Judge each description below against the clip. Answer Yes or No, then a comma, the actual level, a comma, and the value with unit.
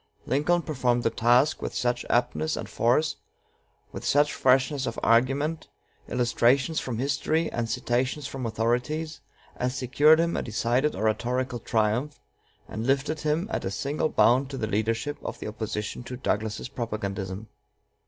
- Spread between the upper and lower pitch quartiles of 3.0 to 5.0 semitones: Yes, average, 4.1 semitones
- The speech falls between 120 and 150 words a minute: Yes, average, 145 wpm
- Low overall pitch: Yes, low, 125 Hz